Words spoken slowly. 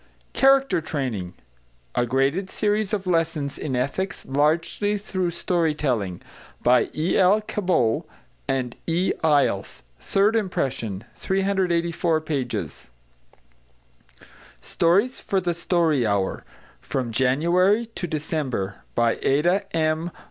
Yes: slow, 105 wpm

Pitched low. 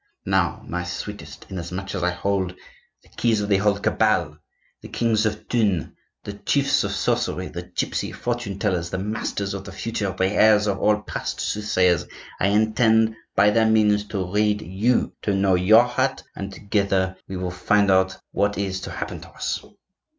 Yes: low, 100 Hz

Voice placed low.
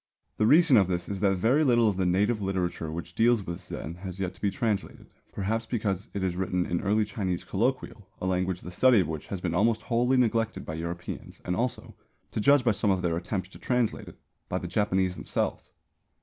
Yes: low, 100 Hz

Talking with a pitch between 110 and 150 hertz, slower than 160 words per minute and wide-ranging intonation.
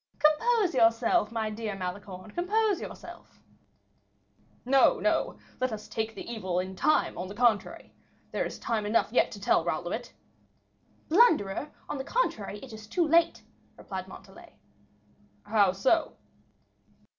No: high, 225 Hz; average, 145 wpm; wide, 7.0 semitones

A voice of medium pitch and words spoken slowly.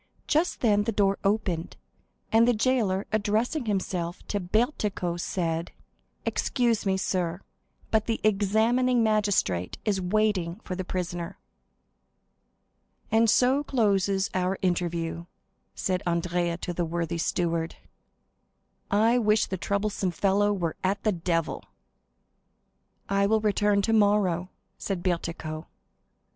No: high, 195 Hz; slow, 115 wpm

